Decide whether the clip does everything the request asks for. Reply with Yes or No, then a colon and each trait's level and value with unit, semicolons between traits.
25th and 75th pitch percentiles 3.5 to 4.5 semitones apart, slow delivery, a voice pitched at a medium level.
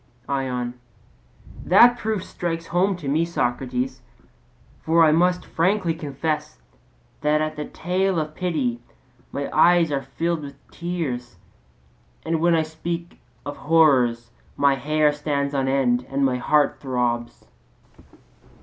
Yes: average, 3.8 semitones; slow, 130 wpm; medium, 150 Hz